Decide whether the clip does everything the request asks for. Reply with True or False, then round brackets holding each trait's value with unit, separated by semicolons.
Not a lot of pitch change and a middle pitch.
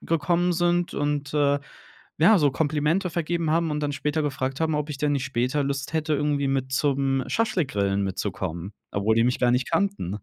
False (3.4 semitones; 145 Hz)